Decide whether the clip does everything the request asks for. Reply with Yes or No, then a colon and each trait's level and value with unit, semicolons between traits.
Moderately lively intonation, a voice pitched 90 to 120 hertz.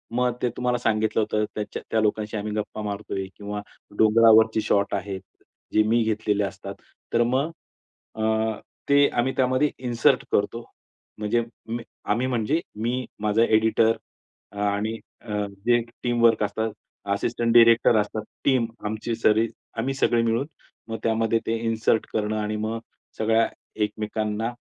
No: narrow, 1.8 semitones; low, 110 Hz